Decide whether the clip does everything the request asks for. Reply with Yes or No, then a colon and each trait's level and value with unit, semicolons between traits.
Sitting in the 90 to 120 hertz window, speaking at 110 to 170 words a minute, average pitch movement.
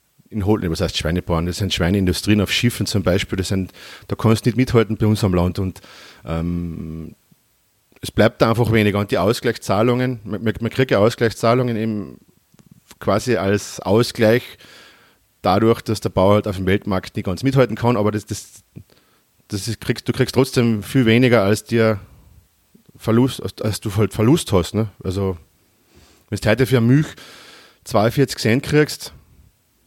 Yes: low, 110 Hz; average, 165 wpm; average, 3.6 semitones